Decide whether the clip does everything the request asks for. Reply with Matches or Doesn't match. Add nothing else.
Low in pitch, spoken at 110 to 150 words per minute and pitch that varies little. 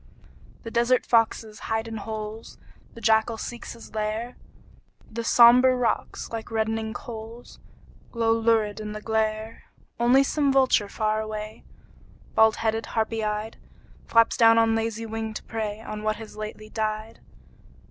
Doesn't match